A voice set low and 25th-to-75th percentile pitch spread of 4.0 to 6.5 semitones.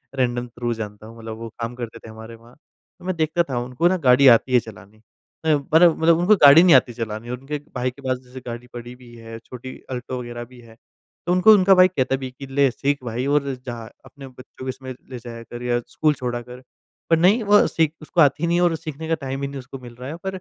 Yes: low, 130 Hz; average, 4.3 semitones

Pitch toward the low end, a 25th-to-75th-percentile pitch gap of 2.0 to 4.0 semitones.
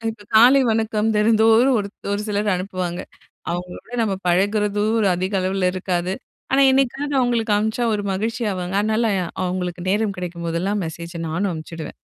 No: high, 205 Hz; average, 3.5 semitones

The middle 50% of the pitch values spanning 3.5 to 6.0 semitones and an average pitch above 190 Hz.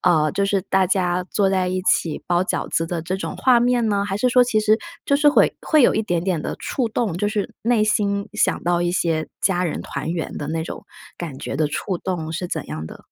No: average, 4.0 semitones; medium, 185 Hz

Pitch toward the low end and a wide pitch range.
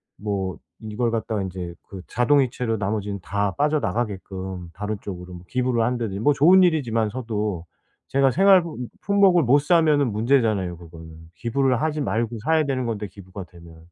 Yes: low, 110 Hz; wide, 6.1 semitones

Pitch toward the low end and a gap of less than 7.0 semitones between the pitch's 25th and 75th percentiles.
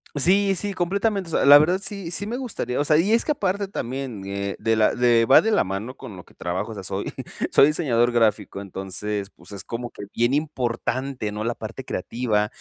No: low, 125 Hz; wide, 8.7 semitones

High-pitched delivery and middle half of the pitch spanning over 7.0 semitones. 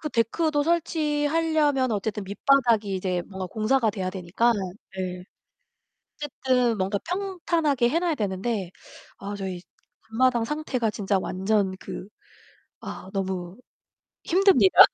Yes: high, 230 Hz; wide, 7.4 semitones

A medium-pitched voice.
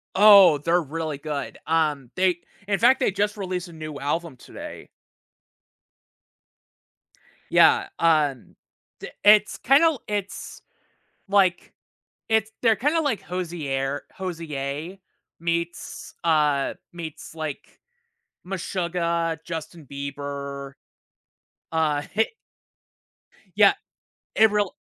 Yes: medium, 170 Hz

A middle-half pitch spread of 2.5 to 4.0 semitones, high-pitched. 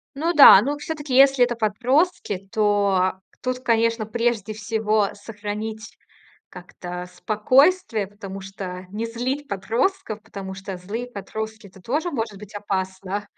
Yes: average, 3.7 semitones; high, 215 Hz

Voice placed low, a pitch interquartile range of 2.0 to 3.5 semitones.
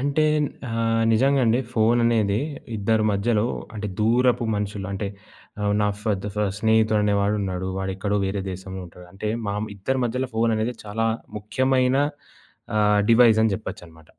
Yes: low, 110 Hz; narrow, 2.5 semitones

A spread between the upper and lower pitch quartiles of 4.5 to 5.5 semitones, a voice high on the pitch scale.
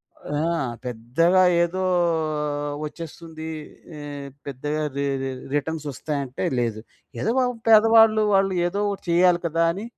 No: average, 4.8 semitones; medium, 165 Hz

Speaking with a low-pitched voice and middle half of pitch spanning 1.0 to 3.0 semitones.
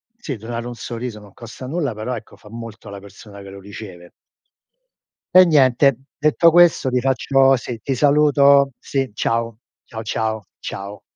No: low, 120 Hz; average, 4.3 semitones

